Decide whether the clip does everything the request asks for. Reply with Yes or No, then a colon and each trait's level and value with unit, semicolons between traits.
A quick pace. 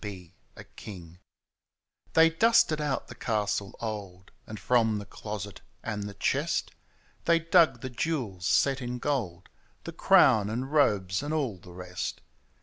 No: average, 160 wpm